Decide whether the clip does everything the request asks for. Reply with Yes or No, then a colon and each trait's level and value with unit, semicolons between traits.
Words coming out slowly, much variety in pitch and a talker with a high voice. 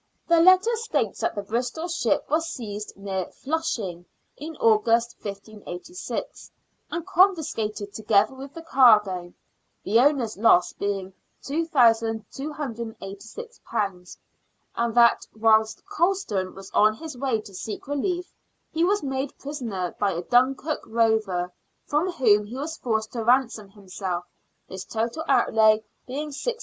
Yes: slow, 130 wpm; wide, 6.3 semitones; high, 230 Hz